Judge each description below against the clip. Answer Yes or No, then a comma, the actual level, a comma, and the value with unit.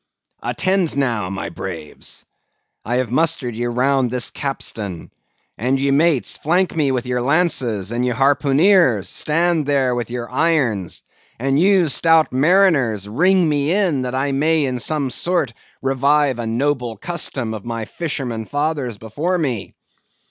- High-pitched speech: No, low, 135 Hz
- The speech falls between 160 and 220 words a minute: No, average, 150 wpm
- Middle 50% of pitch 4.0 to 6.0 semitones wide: Yes, average, 4.8 semitones